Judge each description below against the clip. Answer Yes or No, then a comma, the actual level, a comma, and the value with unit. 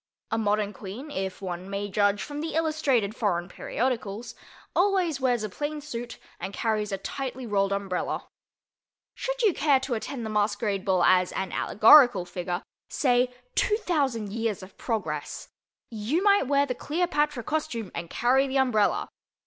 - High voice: Yes, high, 230 Hz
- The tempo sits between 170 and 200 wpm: No, average, 145 wpm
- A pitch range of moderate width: No, wide, 6.0 semitones